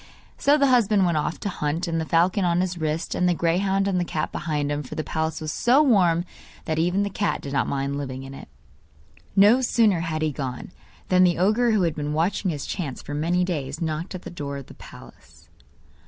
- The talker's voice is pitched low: No, medium, 170 Hz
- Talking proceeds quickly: Yes, fast, 230 wpm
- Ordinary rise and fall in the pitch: Yes, average, 4.0 semitones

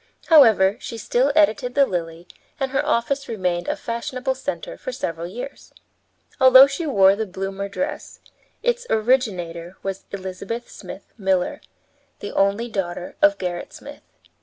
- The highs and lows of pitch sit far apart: Yes, wide, 6.0 semitones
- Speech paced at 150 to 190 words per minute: No, average, 140 wpm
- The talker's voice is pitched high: Yes, high, 220 Hz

